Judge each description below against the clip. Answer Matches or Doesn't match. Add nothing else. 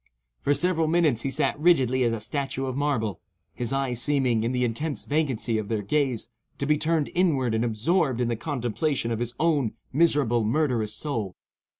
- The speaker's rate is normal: Matches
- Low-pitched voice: Matches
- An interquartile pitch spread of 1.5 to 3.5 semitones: Doesn't match